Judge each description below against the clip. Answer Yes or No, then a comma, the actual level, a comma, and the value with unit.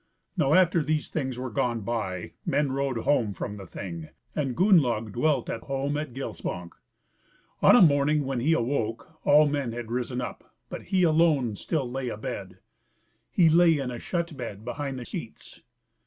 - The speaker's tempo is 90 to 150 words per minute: No, average, 170 wpm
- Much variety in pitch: No, average, 4.6 semitones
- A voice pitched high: No, low, 135 Hz